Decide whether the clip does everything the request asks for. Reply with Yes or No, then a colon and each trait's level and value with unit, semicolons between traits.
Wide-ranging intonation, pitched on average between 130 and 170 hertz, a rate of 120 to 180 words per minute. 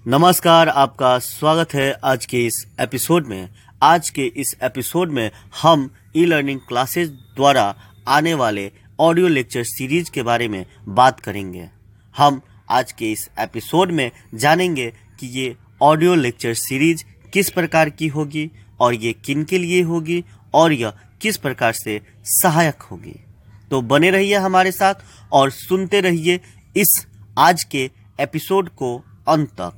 Yes: wide, 7.0 semitones; low, 135 Hz; average, 145 wpm